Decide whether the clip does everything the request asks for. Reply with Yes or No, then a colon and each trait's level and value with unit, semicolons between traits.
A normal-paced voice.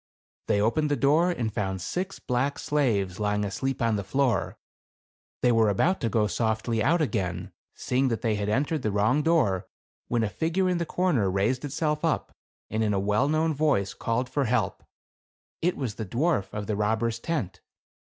Yes: average, 185 wpm